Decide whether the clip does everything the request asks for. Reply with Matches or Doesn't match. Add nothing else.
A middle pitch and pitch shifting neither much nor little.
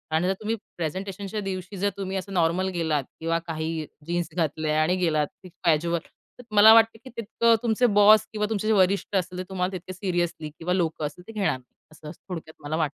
Matches